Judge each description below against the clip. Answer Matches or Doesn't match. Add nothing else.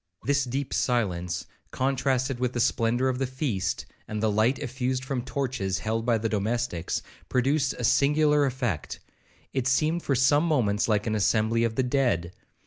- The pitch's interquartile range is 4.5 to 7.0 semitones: Doesn't match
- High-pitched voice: Doesn't match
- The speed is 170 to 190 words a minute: Doesn't match